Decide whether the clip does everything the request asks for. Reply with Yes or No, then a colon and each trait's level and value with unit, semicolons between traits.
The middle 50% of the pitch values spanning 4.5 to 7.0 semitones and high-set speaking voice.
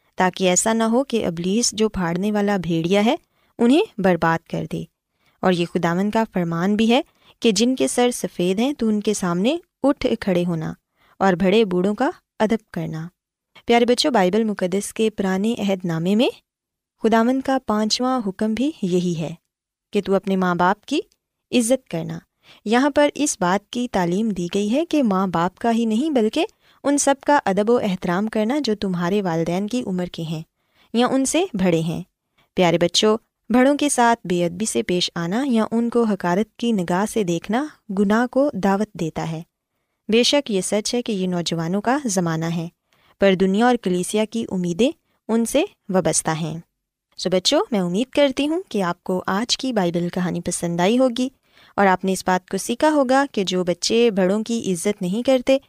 Yes: average, 5.1 semitones; high, 205 Hz